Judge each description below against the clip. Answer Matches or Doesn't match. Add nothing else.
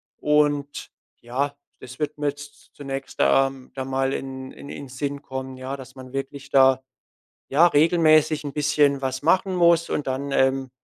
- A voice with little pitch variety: Matches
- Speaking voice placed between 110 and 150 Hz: Matches